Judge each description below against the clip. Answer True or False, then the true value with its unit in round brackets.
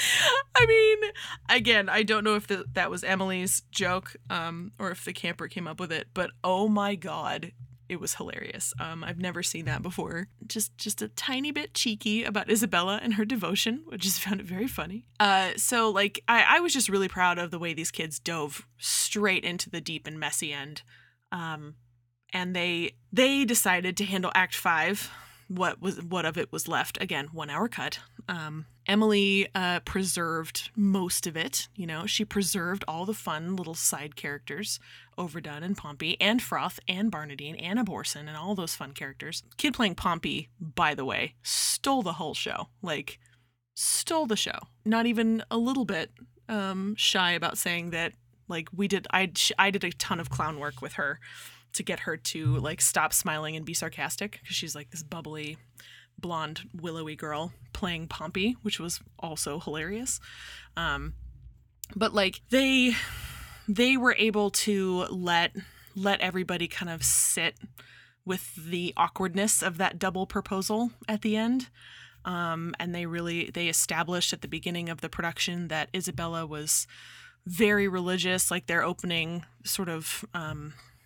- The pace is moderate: True (170 wpm)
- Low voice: False (180 Hz)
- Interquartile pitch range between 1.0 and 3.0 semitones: False (4.1 semitones)